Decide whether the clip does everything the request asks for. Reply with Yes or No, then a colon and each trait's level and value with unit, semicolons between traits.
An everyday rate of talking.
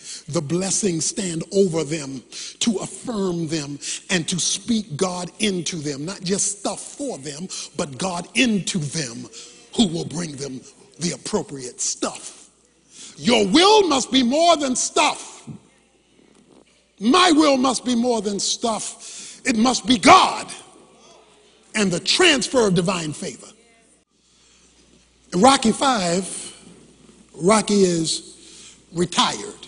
No: slow, 120 wpm